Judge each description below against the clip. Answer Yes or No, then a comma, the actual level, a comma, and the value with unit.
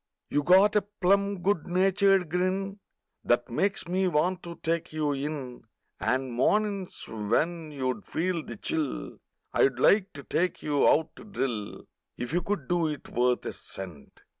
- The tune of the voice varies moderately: No, wide, 5.9 semitones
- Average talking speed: Yes, average, 160 wpm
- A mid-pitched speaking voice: Yes, medium, 165 Hz